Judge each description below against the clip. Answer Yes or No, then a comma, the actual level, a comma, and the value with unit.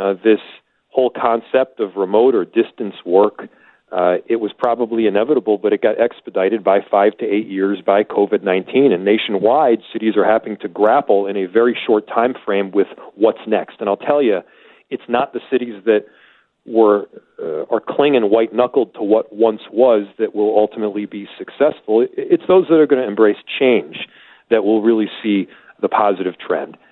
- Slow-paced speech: No, average, 175 wpm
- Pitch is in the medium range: No, low, 115 Hz